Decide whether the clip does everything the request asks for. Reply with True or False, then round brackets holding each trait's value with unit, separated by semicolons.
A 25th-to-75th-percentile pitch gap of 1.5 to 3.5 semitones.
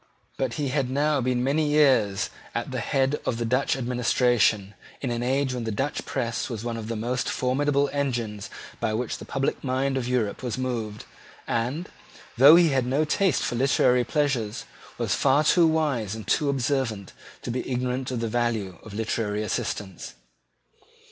True (3.2 semitones)